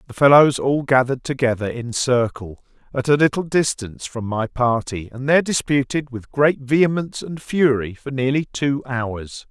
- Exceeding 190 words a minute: No, average, 165 wpm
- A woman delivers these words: No, male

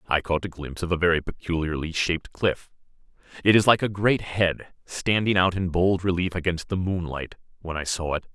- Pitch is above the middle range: No, very low, 90 Hz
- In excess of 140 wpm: Yes, average, 195 wpm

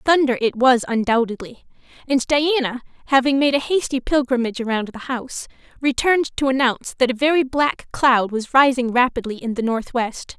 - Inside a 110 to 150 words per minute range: No, average, 160 wpm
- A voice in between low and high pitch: No, very high, 255 Hz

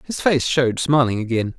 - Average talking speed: Yes, average, 190 wpm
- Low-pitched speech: Yes, low, 130 Hz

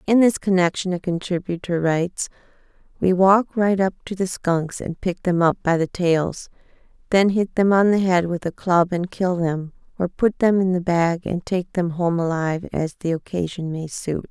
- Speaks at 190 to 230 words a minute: Yes, average, 200 wpm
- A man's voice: No, female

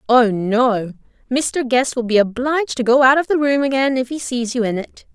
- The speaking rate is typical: No, fast, 235 wpm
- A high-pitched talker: Yes, very high, 250 Hz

